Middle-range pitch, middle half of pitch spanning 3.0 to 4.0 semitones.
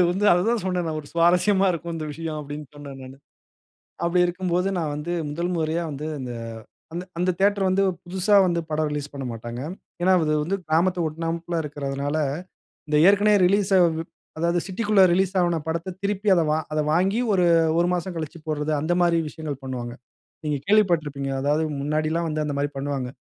Yes: medium, 170 Hz; average, 3.5 semitones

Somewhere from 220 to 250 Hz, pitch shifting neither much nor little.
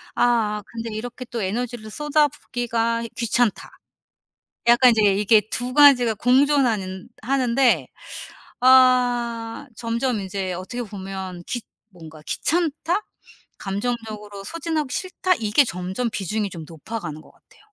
Yes: high, 230 Hz; average, 3.9 semitones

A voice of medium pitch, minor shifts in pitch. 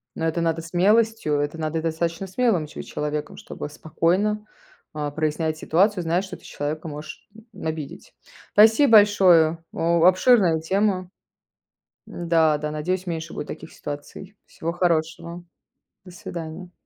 No: medium, 165 Hz; average, 3.0 semitones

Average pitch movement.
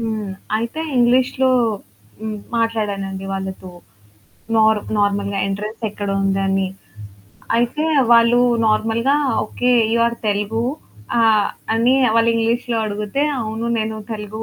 No: narrow, 2.3 semitones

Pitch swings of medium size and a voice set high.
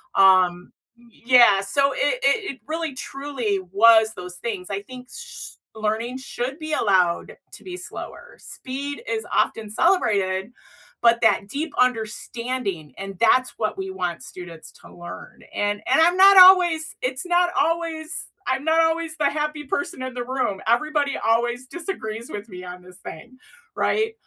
No: wide, 7.4 semitones; very high, 250 Hz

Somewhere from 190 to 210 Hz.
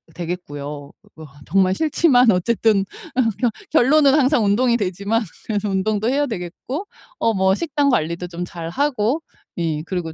Yes: high, 200 Hz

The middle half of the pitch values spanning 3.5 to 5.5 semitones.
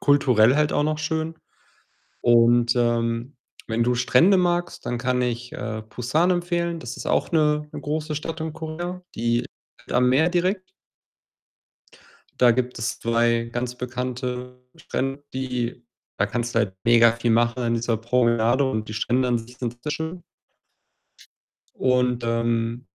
Yes: average, 4.3 semitones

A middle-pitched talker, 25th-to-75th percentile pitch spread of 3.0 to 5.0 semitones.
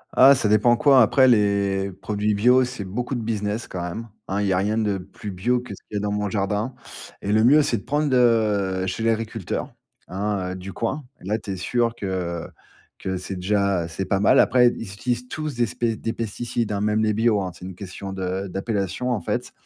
No: low, 105 Hz; average, 3.4 semitones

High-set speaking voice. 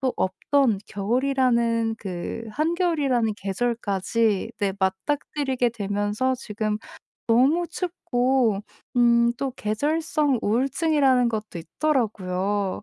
Yes: high, 235 Hz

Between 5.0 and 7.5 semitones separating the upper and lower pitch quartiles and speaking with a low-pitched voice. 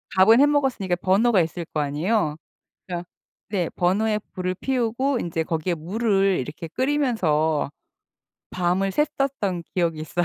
No: wide, 5.4 semitones; medium, 185 Hz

